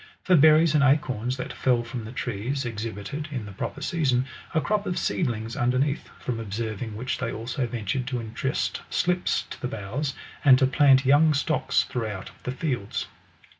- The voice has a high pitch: No, low, 130 Hz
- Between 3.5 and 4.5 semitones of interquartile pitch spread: Yes, average, 4.0 semitones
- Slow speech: No, average, 175 wpm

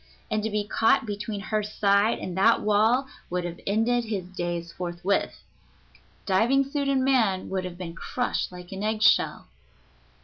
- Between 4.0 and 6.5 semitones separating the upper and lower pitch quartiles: No, average, 3.5 semitones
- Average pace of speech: Yes, average, 165 wpm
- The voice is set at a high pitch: Yes, high, 205 Hz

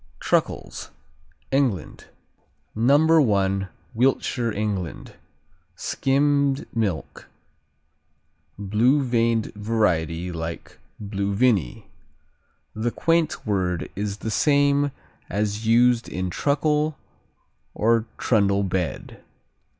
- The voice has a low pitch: Yes, low, 110 Hz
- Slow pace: Yes, slow, 80 wpm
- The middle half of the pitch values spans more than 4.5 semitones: Yes, average, 5.3 semitones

